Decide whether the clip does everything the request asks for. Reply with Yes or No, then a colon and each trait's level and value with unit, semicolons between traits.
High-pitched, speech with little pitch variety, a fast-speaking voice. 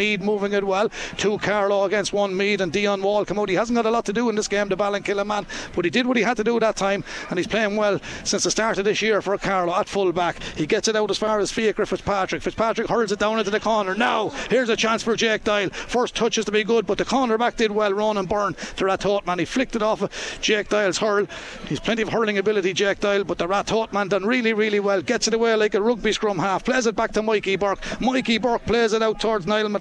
Yes: high, 210 Hz; narrow, 1.9 semitones; fast, 275 wpm